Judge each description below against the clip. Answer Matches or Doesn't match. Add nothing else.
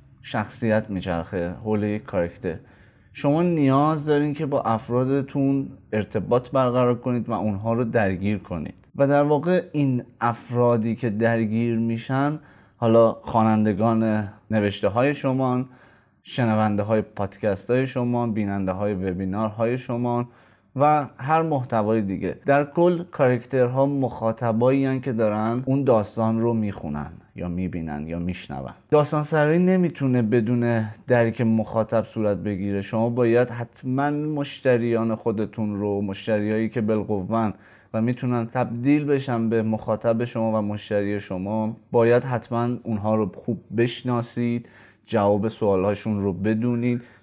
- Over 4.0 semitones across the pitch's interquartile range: Doesn't match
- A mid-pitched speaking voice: Doesn't match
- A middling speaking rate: Matches